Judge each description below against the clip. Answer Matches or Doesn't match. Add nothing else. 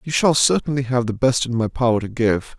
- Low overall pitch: Matches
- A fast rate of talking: Matches